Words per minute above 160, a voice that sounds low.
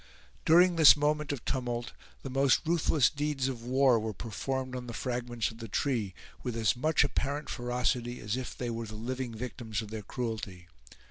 Yes: average, 185 wpm; low, 125 Hz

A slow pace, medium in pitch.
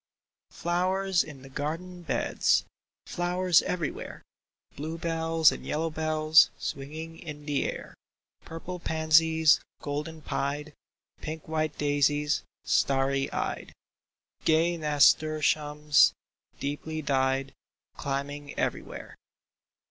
Yes: slow, 95 wpm; medium, 155 Hz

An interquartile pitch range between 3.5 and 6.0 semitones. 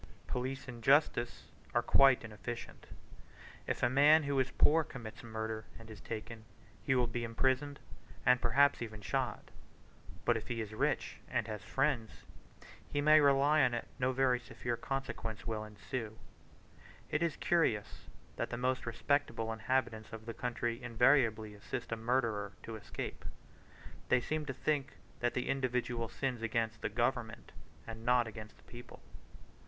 No: average, 3.1 semitones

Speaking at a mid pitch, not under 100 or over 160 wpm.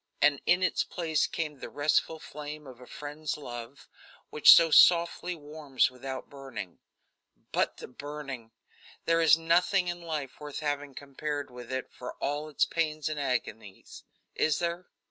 Yes: medium, 150 Hz; average, 155 wpm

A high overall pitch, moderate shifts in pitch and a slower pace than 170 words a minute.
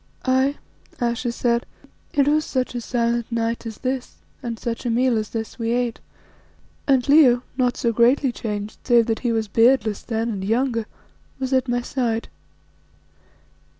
No: high, 240 Hz; narrow, 2.1 semitones; average, 160 wpm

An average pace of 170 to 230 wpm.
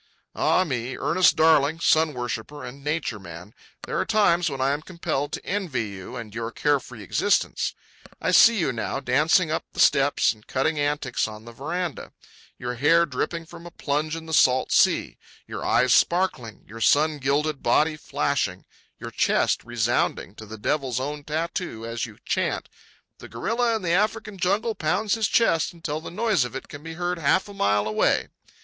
Yes: average, 180 wpm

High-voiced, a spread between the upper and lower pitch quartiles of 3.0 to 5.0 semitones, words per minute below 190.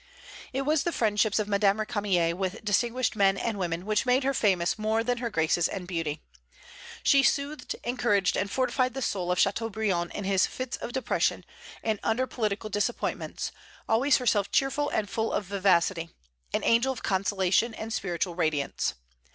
Yes: high, 210 Hz; average, 4.2 semitones; average, 165 wpm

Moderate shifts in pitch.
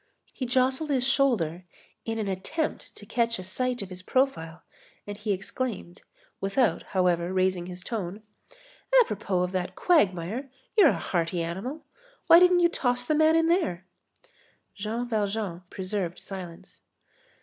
No: wide, 6.0 semitones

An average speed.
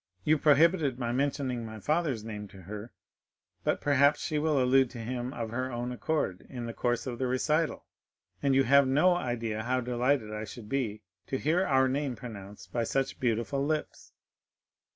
Yes: average, 180 wpm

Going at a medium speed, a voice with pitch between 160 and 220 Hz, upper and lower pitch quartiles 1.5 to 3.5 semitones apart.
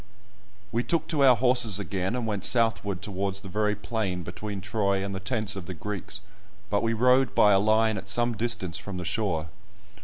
No: average, 195 wpm; low, 105 Hz; average, 2.8 semitones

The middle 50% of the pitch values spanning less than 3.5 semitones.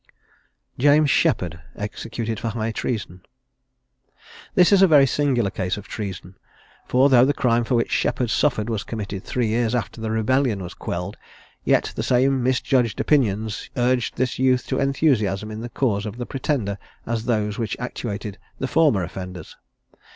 No: average, 3.8 semitones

